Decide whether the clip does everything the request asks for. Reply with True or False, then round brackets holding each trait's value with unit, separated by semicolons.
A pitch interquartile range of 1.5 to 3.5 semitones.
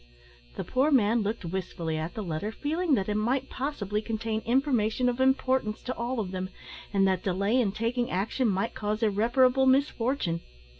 False (4.5 semitones)